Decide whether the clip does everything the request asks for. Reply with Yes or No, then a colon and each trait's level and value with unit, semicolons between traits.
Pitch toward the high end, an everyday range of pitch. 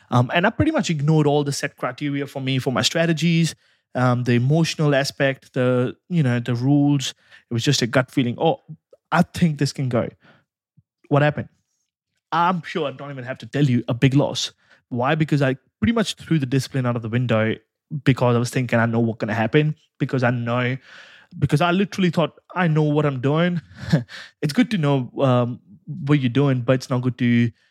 No: medium, 140 Hz; average, 3.9 semitones